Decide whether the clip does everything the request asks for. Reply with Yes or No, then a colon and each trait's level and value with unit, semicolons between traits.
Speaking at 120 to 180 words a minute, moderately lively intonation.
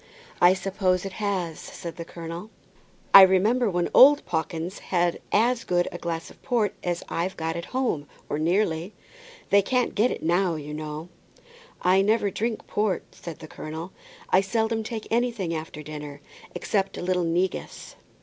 Yes: average, 165 wpm; average, 4.0 semitones